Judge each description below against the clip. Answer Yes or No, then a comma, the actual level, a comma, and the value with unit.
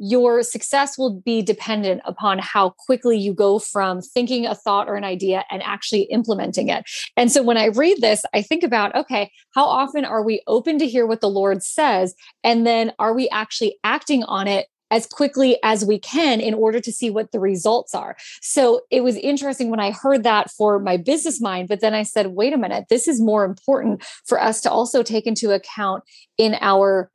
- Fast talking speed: Yes, fast, 210 wpm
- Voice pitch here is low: No, high, 225 Hz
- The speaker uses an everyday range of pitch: Yes, average, 3.7 semitones